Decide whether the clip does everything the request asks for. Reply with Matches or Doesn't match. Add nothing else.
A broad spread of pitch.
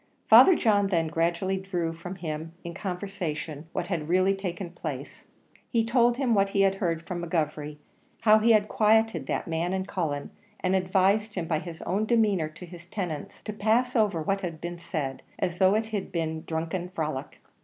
Doesn't match